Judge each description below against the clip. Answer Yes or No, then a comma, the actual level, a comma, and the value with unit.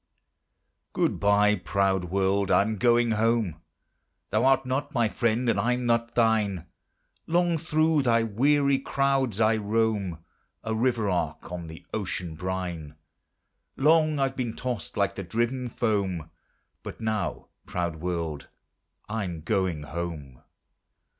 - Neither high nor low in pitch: No, low, 110 Hz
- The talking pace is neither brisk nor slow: No, slow, 125 wpm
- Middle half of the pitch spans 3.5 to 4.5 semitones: No, average, 5.0 semitones